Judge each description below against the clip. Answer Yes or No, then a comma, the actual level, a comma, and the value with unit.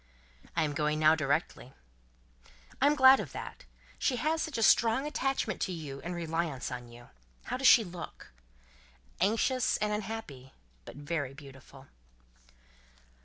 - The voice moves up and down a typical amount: No, wide, 8.4 semitones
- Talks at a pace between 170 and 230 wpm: No, average, 145 wpm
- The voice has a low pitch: No, medium, 170 Hz